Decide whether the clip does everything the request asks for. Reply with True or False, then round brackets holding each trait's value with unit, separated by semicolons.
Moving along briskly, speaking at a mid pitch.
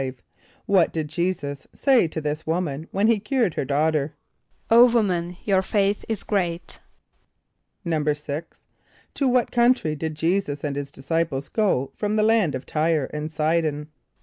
False (150 wpm; 165 Hz)